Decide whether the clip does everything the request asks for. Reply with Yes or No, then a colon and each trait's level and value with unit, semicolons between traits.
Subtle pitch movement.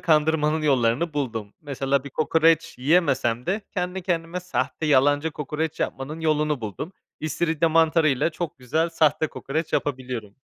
No: average, 3.4 semitones